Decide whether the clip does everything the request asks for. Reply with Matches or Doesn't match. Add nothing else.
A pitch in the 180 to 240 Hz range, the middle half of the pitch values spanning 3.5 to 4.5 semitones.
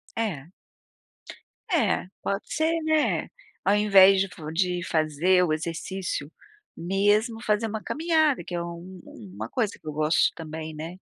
Doesn't match